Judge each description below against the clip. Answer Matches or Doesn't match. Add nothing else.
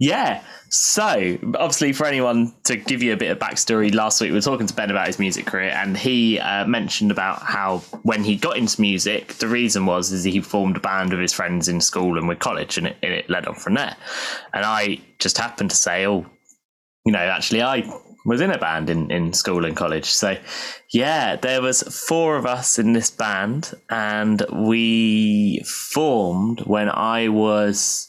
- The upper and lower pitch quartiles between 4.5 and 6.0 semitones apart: Doesn't match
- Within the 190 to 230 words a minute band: Matches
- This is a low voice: Matches